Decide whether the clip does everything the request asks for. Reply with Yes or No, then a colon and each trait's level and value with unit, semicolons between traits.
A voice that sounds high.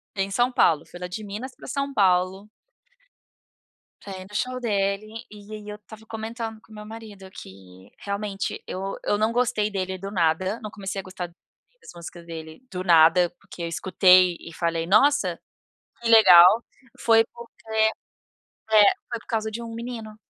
Yes: high, 205 Hz